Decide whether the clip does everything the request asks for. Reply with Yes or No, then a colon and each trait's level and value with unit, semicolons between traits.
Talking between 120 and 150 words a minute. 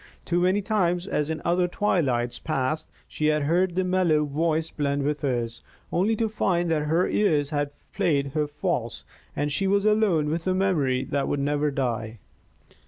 No: average, 175 wpm